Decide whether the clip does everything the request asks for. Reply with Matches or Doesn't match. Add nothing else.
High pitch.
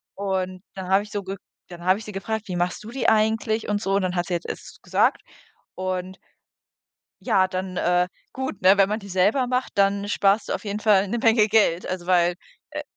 Matches